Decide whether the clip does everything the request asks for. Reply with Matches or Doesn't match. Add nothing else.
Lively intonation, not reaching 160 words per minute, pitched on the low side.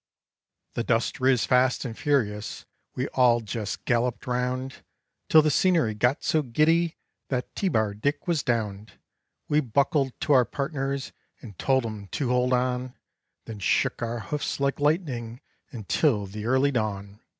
Doesn't match